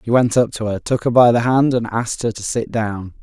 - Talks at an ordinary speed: No, fast, 295 wpm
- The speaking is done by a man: Yes, male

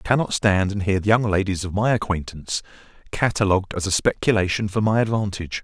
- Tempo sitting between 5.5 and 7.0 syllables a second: Yes, 6.4 syllables/s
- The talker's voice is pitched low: Yes, low, 100 Hz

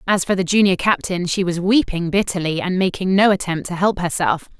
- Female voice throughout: Yes, female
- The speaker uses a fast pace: Yes, fast, 210 wpm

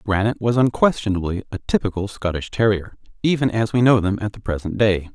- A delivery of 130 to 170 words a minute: No, average, 185 wpm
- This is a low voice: Yes, low, 105 Hz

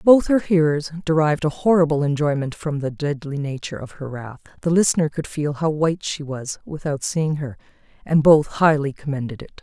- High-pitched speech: No, medium, 150 Hz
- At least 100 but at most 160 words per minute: No, average, 175 wpm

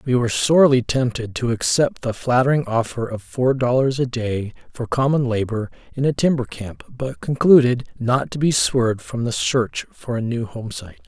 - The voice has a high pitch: No, low, 125 Hz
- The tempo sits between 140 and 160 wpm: No, average, 185 wpm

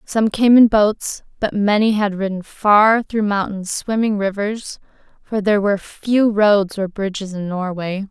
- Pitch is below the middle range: No, high, 205 Hz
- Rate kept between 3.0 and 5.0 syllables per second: Yes, 4.2 syllables/s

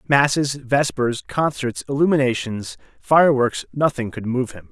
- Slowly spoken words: Yes, slow, 115 wpm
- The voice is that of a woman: No, male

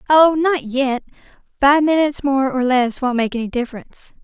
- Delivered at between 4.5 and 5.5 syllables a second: Yes, 5.4 syllables/s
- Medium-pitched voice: No, very high, 270 Hz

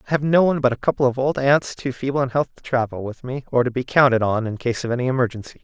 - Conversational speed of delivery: No, fast, 300 wpm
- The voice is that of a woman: No, male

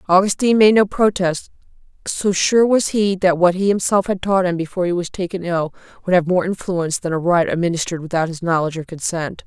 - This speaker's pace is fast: Yes, fast, 210 wpm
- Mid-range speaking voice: Yes, medium, 180 Hz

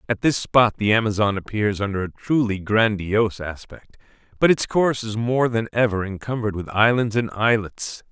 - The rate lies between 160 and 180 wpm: Yes, average, 170 wpm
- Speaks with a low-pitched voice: Yes, low, 110 Hz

